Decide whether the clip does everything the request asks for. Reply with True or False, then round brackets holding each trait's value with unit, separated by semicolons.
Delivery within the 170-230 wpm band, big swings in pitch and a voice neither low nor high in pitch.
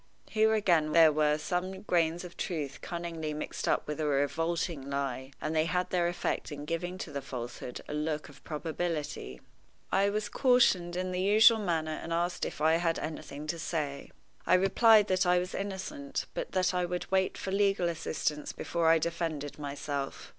False (180 wpm; 3.4 semitones; 170 Hz)